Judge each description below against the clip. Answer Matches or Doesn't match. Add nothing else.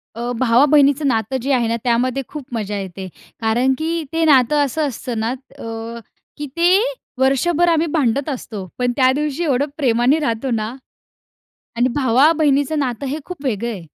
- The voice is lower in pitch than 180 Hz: Doesn't match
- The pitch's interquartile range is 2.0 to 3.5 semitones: Doesn't match